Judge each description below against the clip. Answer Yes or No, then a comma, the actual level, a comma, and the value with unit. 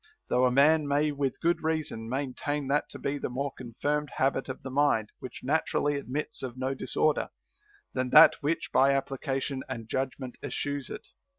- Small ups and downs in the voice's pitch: Yes, narrow, 2.1 semitones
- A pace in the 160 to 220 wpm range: Yes, average, 175 wpm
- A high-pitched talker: No, medium, 140 Hz